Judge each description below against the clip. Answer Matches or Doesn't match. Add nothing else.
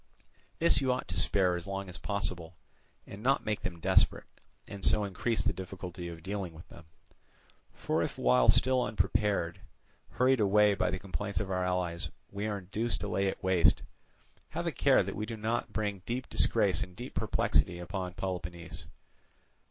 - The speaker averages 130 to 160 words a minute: Doesn't match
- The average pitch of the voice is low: Matches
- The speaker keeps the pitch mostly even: Doesn't match